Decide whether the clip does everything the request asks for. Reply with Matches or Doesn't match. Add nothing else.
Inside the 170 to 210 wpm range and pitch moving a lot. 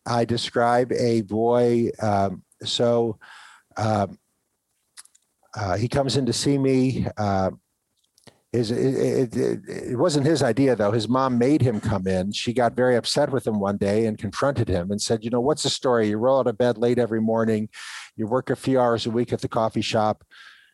Doesn't match